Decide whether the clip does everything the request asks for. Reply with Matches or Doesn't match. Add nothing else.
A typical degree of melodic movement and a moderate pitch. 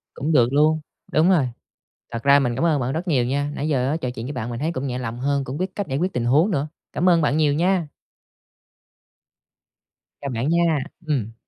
Matches